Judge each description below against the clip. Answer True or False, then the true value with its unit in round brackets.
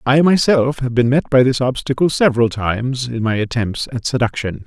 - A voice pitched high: False (125 Hz)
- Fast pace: False (195 wpm)